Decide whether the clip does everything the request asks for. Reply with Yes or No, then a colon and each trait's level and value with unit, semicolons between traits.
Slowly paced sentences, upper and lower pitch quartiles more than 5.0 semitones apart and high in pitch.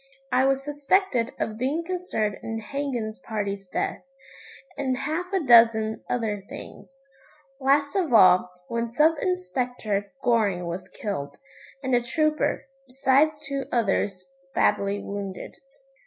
Yes: slow, 125 wpm; wide, 5.5 semitones; high, 240 Hz